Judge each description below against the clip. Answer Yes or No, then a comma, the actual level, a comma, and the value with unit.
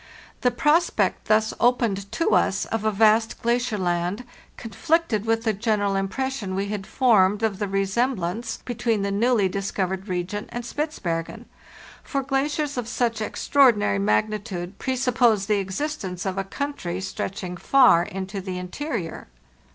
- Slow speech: No, average, 145 wpm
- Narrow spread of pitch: No, average, 4.2 semitones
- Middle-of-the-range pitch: No, high, 210 Hz